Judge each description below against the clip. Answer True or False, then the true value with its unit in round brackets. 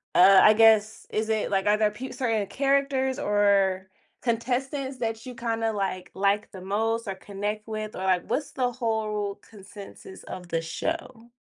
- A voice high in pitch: True (215 Hz)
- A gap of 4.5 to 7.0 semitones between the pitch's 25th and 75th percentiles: False (3.1 semitones)